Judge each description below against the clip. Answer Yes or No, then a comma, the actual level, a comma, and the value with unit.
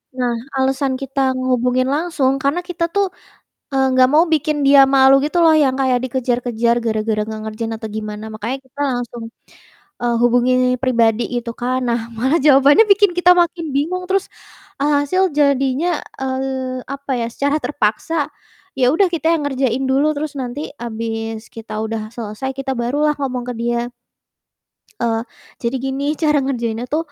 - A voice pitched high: Yes, very high, 265 Hz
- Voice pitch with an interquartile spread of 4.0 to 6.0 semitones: No, average, 3.6 semitones